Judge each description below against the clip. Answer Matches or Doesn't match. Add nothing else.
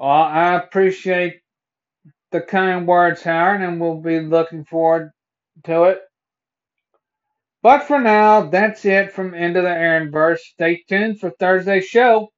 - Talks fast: Doesn't match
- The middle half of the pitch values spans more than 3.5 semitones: Doesn't match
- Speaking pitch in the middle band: Matches